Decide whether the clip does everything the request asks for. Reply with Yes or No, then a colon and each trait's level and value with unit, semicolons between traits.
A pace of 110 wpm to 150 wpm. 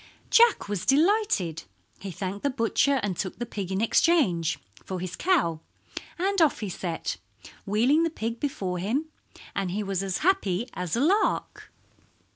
No: average, 160 wpm